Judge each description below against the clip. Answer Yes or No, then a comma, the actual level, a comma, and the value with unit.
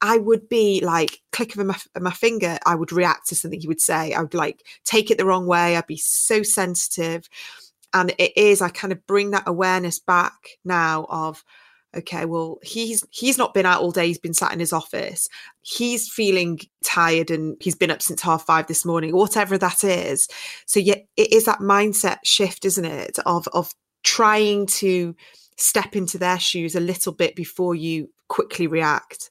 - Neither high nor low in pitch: Yes, medium, 180 Hz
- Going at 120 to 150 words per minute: No, average, 195 wpm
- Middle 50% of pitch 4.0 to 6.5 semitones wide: No, average, 3.6 semitones